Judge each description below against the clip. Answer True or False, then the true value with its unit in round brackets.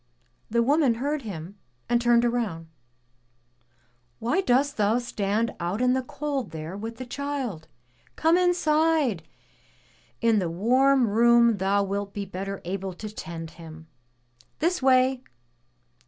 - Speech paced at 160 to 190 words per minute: False (135 wpm)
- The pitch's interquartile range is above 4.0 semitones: True (5.2 semitones)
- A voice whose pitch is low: False (230 Hz)